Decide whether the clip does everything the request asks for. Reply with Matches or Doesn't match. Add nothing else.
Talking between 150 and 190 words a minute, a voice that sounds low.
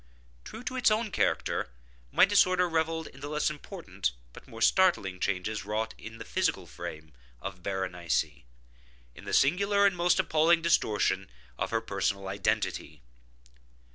Doesn't match